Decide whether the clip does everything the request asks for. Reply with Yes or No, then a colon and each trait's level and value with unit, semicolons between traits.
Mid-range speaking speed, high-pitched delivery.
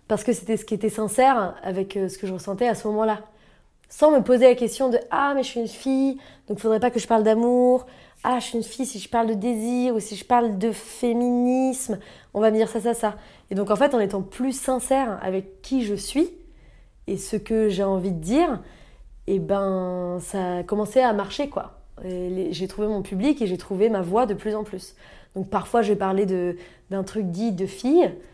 No: fast, 235 wpm; high, 220 Hz